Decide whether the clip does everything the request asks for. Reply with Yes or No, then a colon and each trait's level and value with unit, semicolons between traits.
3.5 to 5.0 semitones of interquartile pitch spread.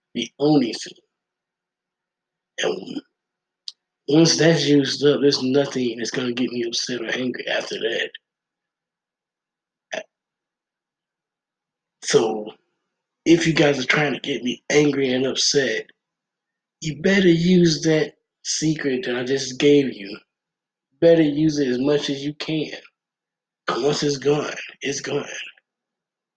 Yes: average, 3.8 semitones